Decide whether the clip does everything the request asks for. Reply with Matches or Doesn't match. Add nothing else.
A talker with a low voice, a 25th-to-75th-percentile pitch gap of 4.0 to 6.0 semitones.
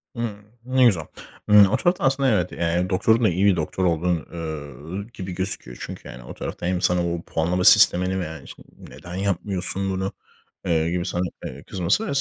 Doesn't match